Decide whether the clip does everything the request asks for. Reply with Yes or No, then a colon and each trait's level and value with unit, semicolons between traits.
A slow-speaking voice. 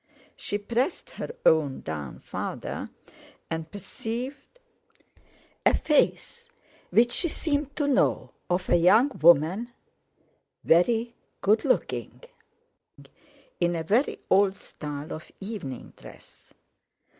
Yes: slow, 105 wpm